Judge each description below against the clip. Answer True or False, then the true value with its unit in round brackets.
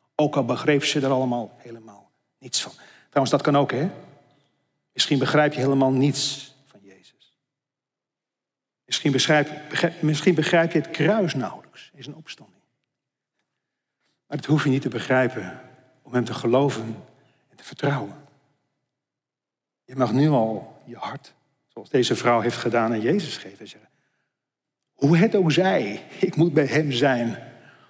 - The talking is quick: False (155 wpm)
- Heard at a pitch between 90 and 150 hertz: True (140 Hz)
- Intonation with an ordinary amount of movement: True (3.0 semitones)